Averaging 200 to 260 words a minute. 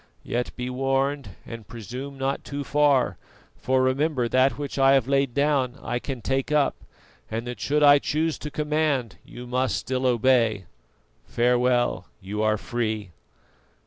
No: average, 150 wpm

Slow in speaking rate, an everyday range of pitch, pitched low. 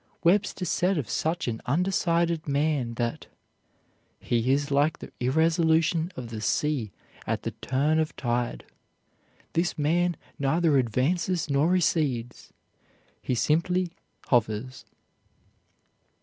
No: slow, 110 wpm; average, 4.8 semitones; medium, 150 Hz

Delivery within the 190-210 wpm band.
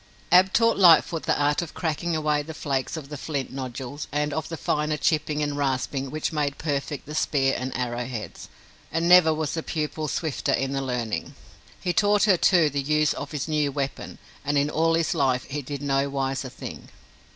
Yes: average, 195 wpm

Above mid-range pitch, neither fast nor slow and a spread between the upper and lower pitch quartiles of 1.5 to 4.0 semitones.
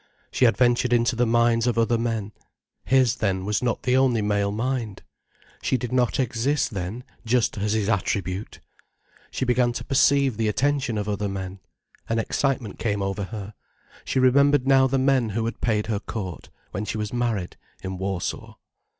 No: low, 115 Hz; average, 175 wpm; average, 3.4 semitones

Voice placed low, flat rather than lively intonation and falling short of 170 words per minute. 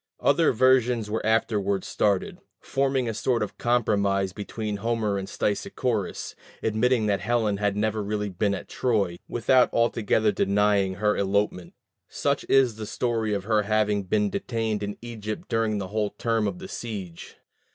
Yes: low, 105 Hz; narrow, 2.3 semitones; average, 155 wpm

